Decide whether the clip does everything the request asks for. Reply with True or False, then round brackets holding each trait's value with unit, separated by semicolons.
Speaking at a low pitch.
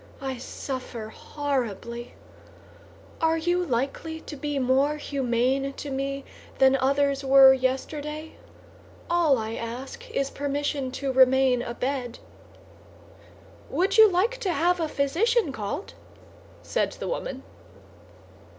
False (275 Hz)